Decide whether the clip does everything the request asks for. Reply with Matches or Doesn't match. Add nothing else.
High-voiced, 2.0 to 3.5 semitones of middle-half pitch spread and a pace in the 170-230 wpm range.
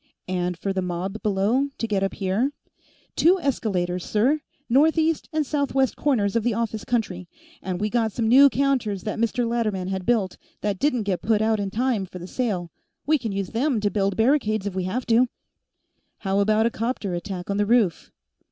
Doesn't match